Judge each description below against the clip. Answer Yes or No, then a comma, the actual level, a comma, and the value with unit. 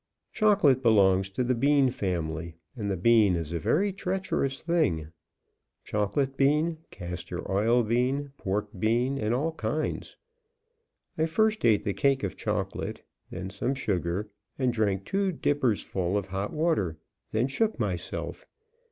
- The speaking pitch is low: Yes, low, 115 Hz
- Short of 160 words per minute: Yes, average, 140 wpm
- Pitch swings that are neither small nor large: No, wide, 6.6 semitones